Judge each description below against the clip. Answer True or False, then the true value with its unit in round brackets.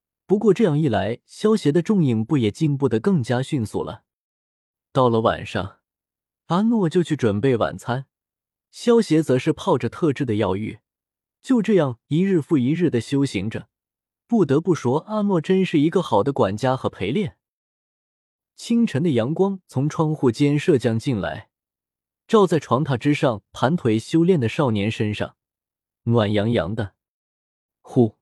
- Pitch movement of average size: False (7.5 semitones)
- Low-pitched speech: True (130 Hz)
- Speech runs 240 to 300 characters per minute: False (225 characters per minute)